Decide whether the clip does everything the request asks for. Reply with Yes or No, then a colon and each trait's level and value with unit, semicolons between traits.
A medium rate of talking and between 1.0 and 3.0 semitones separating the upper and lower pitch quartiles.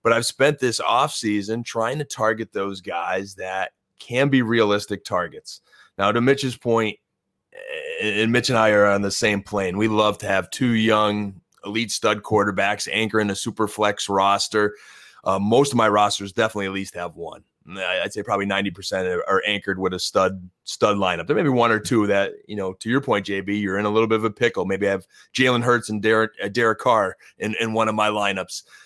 No: fast, 210 wpm; narrow, 2.4 semitones